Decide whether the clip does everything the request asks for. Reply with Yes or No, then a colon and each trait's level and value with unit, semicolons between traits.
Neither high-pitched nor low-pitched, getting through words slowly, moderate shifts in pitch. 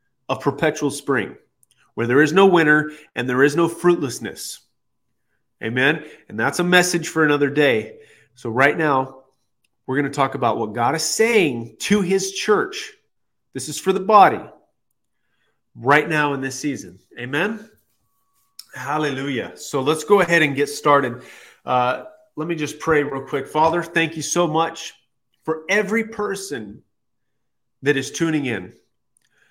No: medium, 145 Hz; average, 150 wpm; average, 4.6 semitones